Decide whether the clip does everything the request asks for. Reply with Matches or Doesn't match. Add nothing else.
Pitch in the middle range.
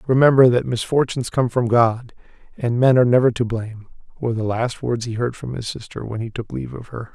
Doesn't match